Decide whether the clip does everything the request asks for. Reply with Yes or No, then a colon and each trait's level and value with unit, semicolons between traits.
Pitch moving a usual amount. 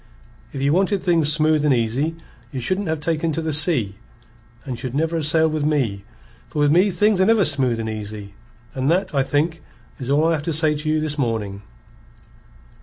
Yes: average, 3.8 semitones